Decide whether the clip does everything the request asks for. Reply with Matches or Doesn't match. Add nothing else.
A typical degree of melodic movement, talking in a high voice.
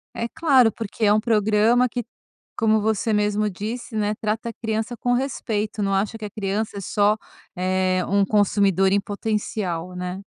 Doesn't match